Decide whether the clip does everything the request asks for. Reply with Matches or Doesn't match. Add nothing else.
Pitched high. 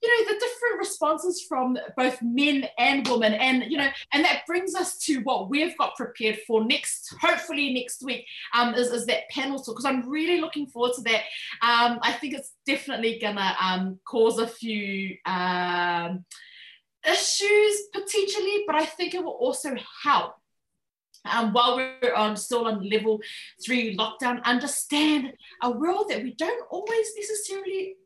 Matches